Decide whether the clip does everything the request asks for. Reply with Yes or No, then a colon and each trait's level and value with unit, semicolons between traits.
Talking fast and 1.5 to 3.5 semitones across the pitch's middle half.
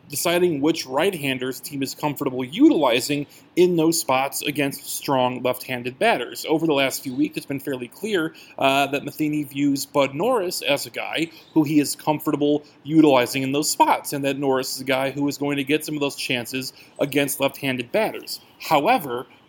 No: average, 180 wpm; narrow, 2.4 semitones